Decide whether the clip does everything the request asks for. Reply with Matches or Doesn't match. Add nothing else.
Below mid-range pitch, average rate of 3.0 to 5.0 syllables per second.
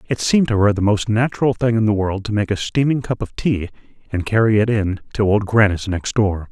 Doesn't match